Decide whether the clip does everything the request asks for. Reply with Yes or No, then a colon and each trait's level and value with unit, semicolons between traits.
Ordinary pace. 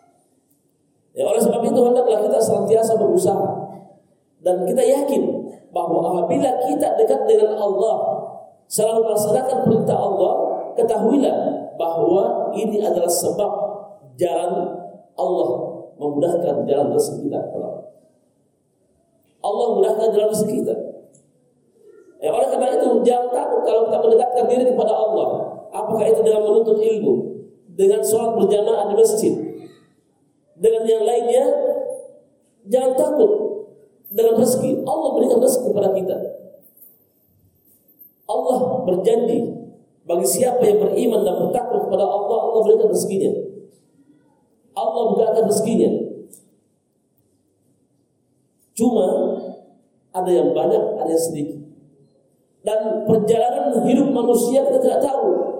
Yes: average, 110 wpm